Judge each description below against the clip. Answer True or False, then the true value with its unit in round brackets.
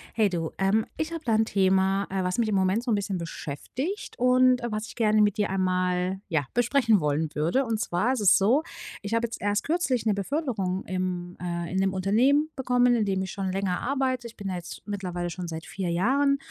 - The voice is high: True (200 Hz)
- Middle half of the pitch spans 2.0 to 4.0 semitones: False (4.8 semitones)